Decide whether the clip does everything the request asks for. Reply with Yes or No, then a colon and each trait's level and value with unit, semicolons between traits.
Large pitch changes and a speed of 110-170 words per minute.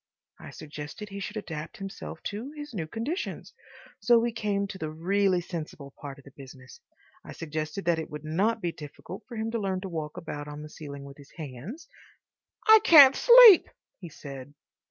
No: wide, 6.6 semitones; average, 190 wpm